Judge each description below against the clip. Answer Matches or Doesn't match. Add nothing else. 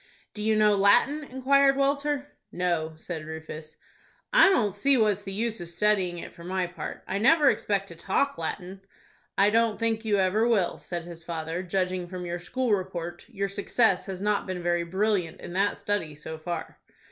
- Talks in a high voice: Matches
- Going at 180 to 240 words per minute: Matches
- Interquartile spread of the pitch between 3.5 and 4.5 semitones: Matches